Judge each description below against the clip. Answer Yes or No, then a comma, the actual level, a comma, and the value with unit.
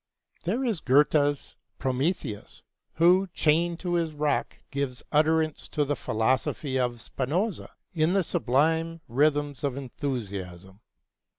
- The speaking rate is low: Yes, slow, 115 wpm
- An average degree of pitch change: Yes, average, 4.1 semitones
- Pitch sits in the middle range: Yes, medium, 145 Hz